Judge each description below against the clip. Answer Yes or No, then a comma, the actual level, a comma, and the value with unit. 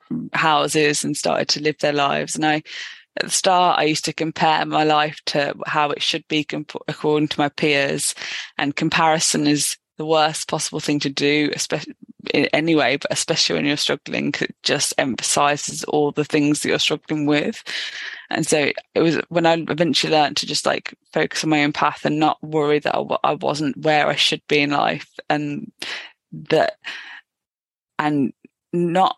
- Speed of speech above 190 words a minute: No, average, 180 wpm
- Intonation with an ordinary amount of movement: No, narrow, 1.3 semitones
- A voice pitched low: No, medium, 150 Hz